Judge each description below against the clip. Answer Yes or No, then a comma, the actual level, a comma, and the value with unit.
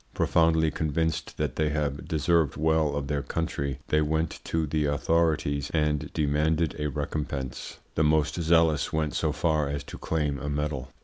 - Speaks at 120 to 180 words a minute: Yes, average, 165 wpm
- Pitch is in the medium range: No, very low, 75 Hz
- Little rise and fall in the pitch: Yes, narrow, 1.8 semitones